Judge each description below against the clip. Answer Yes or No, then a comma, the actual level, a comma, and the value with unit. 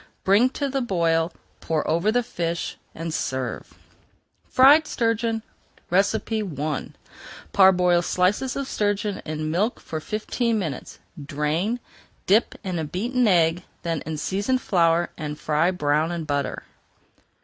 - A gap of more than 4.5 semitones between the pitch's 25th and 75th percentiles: Yes, wide, 5.4 semitones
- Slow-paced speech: Yes, slow, 125 wpm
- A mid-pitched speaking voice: Yes, medium, 180 Hz